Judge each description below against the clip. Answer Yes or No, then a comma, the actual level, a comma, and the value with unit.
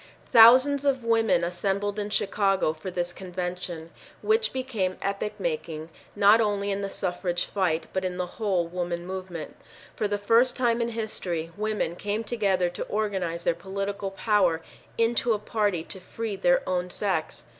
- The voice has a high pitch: Yes, high, 195 Hz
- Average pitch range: Yes, average, 3.3 semitones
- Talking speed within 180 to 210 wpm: No, average, 160 wpm